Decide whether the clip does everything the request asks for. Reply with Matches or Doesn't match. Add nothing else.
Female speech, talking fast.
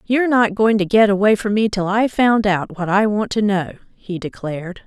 Matches